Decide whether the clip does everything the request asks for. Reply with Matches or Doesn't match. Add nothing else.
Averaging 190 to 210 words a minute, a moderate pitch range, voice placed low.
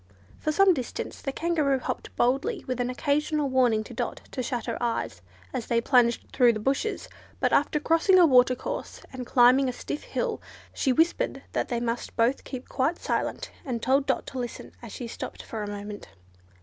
Doesn't match